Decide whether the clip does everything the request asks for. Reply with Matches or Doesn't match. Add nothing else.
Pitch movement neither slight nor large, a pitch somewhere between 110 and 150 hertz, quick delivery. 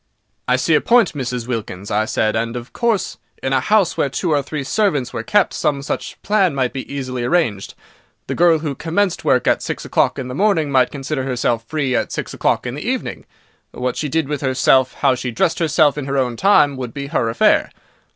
Matches